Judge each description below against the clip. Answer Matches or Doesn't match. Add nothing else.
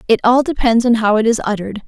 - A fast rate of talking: Matches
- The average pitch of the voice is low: Doesn't match